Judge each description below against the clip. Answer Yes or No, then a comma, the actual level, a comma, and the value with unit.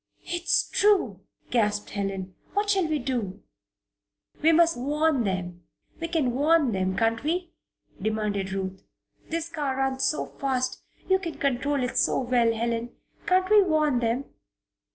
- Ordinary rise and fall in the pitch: No, wide, 6.7 semitones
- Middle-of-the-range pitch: No, very high, 260 Hz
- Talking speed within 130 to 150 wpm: Yes, average, 140 wpm